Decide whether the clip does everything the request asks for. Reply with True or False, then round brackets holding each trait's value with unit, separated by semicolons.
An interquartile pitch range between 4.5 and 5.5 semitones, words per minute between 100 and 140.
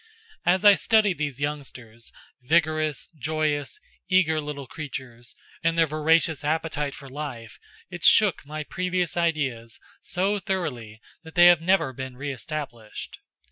False (4.1 semitones; 135 wpm)